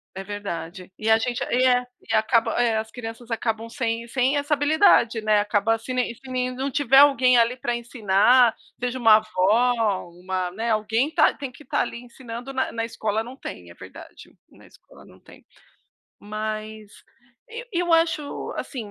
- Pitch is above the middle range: Yes, high, 230 Hz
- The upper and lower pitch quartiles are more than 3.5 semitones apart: No, average, 3.0 semitones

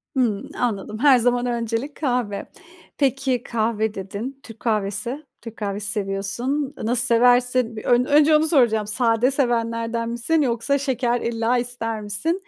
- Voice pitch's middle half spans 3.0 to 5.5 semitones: No, narrow, 2.6 semitones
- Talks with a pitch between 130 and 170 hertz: No, high, 235 Hz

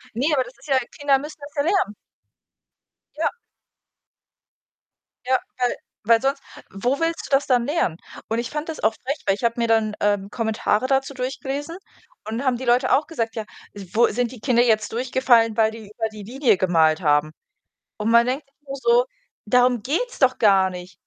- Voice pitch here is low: No, high, 245 Hz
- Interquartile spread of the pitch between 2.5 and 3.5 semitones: No, average, 4.0 semitones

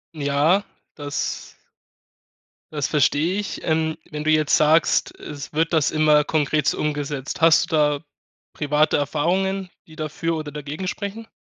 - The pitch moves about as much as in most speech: No, narrow, 1.9 semitones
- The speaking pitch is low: No, medium, 155 Hz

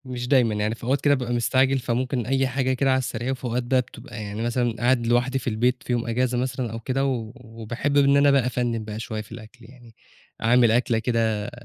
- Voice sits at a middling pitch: No, low, 125 Hz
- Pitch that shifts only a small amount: Yes, narrow, 2.2 semitones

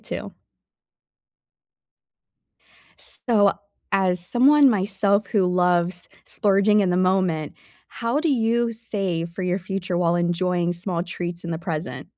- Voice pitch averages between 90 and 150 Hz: No, medium, 185 Hz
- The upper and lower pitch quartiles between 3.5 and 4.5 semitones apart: No, average, 3.1 semitones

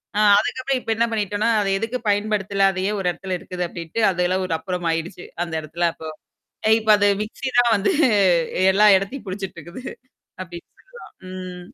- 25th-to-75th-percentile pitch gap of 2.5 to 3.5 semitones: Yes, average, 3.1 semitones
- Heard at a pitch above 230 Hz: No, high, 195 Hz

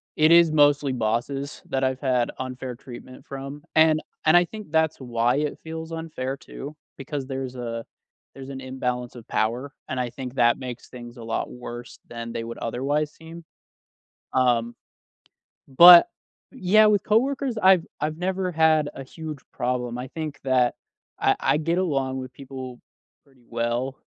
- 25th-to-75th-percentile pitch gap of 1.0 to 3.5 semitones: No, average, 4.3 semitones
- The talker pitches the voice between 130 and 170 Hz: Yes, low, 135 Hz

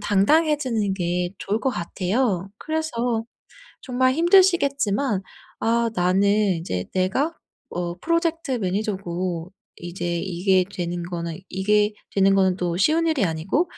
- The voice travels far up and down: Yes, wide, 6.4 semitones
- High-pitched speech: Yes, high, 200 Hz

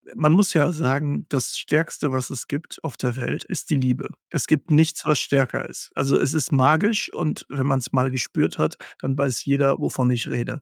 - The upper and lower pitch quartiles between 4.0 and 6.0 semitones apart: No, average, 2.8 semitones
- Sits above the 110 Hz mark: Yes, medium, 140 Hz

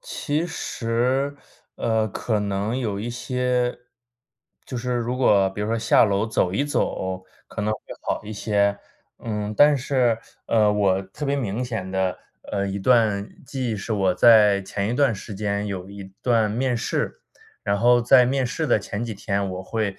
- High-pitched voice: No, low, 110 Hz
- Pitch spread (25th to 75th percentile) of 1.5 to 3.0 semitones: No, average, 3.6 semitones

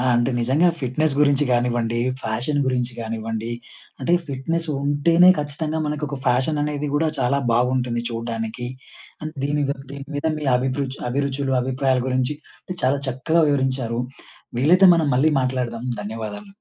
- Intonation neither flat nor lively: Yes, average, 3.3 semitones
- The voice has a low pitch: Yes, low, 130 Hz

